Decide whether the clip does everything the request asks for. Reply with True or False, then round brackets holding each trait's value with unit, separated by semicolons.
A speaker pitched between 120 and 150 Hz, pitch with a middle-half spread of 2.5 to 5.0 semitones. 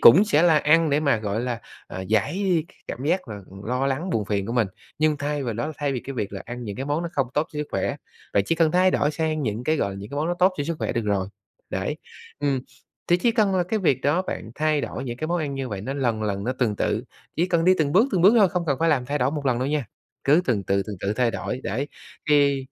False (140 Hz; 5.5 semitones)